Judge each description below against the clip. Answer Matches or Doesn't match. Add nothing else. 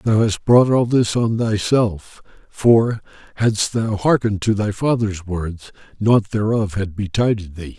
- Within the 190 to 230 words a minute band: Doesn't match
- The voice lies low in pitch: Matches